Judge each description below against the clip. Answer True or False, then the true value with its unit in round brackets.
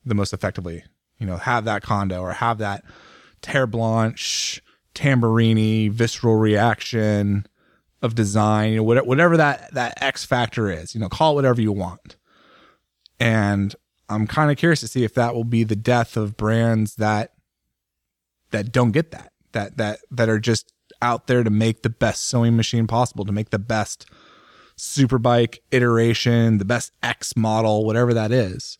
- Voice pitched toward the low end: True (115 Hz)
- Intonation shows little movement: True (2.2 semitones)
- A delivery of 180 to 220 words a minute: False (165 wpm)